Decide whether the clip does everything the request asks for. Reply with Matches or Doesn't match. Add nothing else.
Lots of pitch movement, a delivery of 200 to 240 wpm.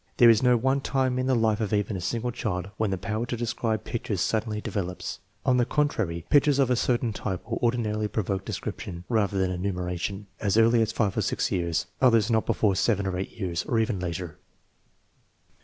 Doesn't match